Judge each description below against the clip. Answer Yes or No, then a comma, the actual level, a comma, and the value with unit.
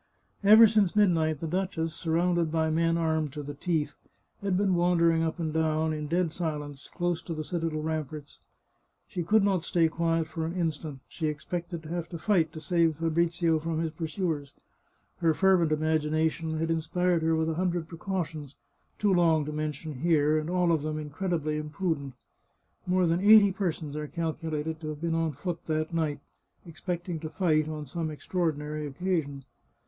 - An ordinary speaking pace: Yes, average, 175 wpm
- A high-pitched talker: No, medium, 160 Hz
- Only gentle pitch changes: Yes, narrow, 2.1 semitones